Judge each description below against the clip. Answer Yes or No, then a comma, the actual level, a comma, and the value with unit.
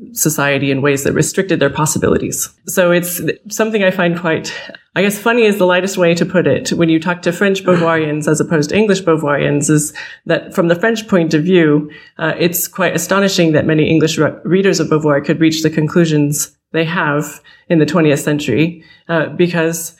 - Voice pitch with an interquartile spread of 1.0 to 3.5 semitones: Yes, average, 2.8 semitones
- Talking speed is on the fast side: No, average, 195 wpm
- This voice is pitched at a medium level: Yes, medium, 165 Hz